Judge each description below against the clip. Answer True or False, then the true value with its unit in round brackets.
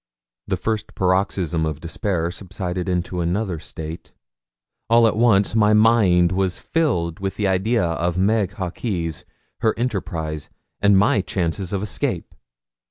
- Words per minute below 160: True (135 wpm)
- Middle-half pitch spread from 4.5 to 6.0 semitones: False (3.5 semitones)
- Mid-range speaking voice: False (95 Hz)